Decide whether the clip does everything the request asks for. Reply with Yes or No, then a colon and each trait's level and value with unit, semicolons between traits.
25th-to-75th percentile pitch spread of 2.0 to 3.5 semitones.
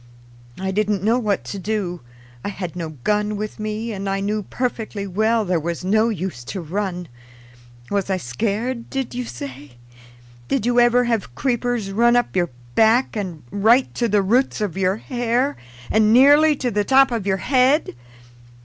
No: average, 4.0 semitones